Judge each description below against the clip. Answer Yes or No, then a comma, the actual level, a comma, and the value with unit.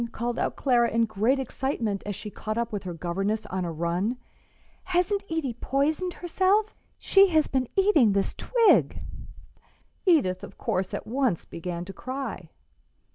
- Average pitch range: No, wide, 8.1 semitones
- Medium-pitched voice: No, high, 235 Hz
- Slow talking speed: No, average, 155 wpm